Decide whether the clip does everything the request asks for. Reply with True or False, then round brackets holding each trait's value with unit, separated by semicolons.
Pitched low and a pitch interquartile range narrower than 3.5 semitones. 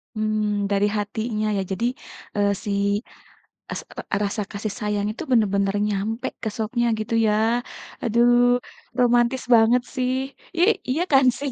False (220 Hz; 2.8 semitones)